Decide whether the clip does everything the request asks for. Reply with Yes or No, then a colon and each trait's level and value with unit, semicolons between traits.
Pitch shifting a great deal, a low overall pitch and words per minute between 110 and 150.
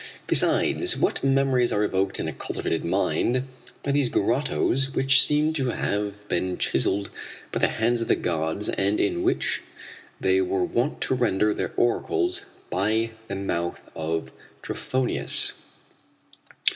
Yes: wide, 5.8 semitones; low, 115 Hz; average, 140 wpm